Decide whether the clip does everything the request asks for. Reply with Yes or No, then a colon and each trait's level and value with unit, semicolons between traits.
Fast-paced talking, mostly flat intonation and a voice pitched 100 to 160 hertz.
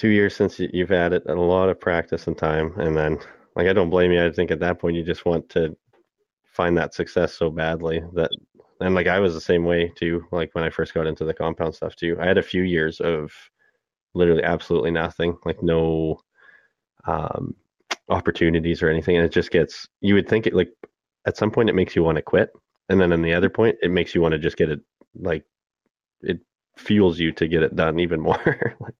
No: fast, 230 wpm; narrow, 2.0 semitones; very low, 85 Hz